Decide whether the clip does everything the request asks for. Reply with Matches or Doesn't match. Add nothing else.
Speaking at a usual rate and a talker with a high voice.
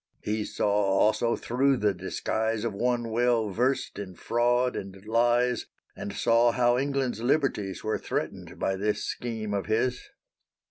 Doesn't match